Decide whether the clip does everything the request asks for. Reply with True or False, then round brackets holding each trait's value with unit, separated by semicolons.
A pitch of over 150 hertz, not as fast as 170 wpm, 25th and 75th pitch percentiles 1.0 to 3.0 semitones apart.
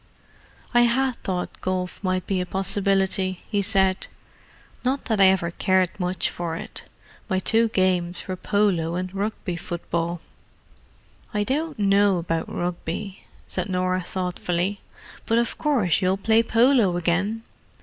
True (190 Hz; 140 wpm; 2.7 semitones)